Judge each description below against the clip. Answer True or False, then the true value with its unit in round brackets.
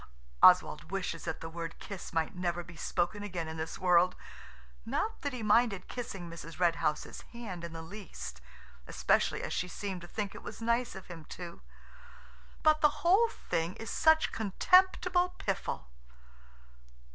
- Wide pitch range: True (5.8 semitones)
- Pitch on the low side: False (185 Hz)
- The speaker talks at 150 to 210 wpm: True (160 wpm)